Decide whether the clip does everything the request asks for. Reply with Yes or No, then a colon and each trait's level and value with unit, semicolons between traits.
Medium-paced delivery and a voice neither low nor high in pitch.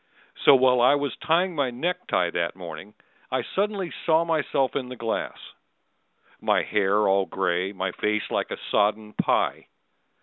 No: average, 160 wpm; low, 120 Hz